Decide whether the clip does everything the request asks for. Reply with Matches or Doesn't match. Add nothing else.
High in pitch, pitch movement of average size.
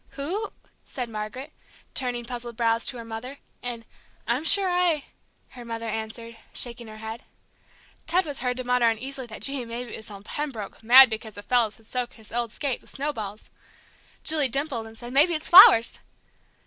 Matches